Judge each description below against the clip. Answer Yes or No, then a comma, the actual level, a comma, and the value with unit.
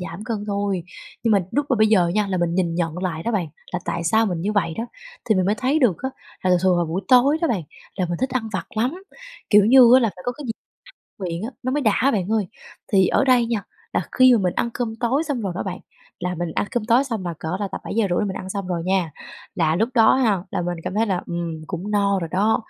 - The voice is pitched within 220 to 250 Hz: No, high, 200 Hz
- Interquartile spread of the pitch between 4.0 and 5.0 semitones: Yes, average, 4.5 semitones